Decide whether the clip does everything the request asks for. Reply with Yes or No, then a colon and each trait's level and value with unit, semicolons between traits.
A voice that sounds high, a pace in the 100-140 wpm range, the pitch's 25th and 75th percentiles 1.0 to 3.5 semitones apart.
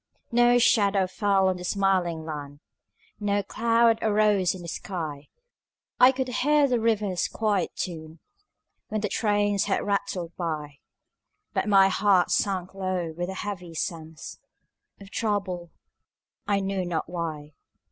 Yes: high, 195 Hz; slow, 135 wpm; average, 3.2 semitones